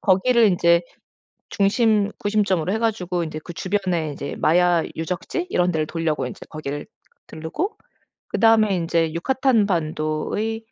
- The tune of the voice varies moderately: Yes, average, 4.7 semitones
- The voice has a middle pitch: Yes, medium, 180 Hz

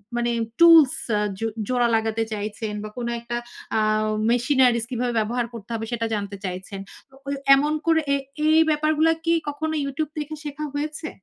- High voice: Yes, very high, 250 Hz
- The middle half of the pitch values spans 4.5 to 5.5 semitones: Yes, average, 5.2 semitones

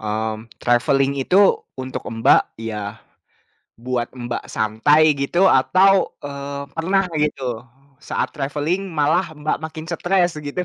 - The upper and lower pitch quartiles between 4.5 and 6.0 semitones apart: Yes, average, 5.1 semitones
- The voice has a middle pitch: Yes, medium, 145 Hz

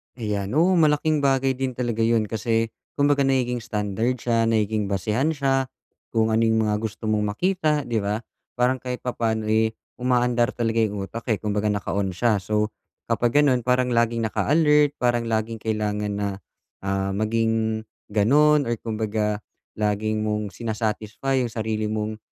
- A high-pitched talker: No, low, 115 Hz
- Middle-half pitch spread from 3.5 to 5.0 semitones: No, average, 2.8 semitones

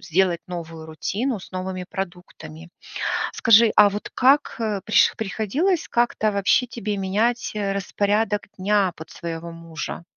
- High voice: Yes, high, 200 Hz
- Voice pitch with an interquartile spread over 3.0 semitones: Yes, average, 3.7 semitones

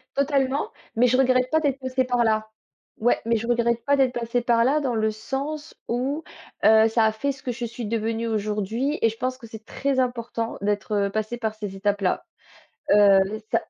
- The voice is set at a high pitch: Yes, high, 235 Hz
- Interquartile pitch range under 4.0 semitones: Yes, average, 3.0 semitones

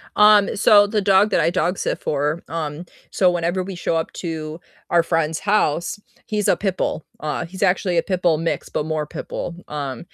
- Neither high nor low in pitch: Yes, medium, 175 Hz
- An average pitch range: Yes, average, 3.5 semitones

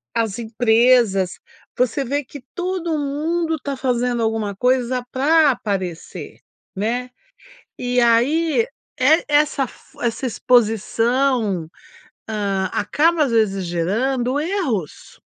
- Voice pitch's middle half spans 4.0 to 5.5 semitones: Yes, average, 4.5 semitones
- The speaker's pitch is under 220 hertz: No, high, 245 Hz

